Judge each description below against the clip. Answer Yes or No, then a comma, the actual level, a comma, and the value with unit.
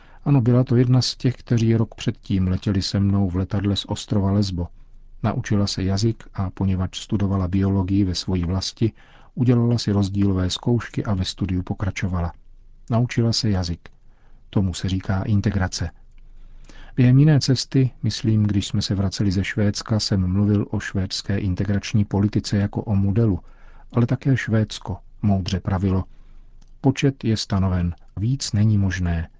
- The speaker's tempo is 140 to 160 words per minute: Yes, average, 145 wpm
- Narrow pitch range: No, average, 3.3 semitones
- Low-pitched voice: Yes, low, 100 Hz